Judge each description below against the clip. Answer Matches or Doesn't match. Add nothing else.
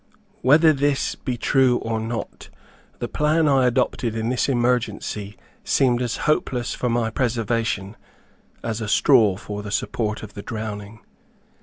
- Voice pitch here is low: Matches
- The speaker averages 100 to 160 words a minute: Matches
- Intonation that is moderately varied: Matches